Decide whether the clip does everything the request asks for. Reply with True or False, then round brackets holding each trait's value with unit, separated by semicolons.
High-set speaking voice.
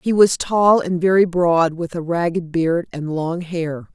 False (170 Hz)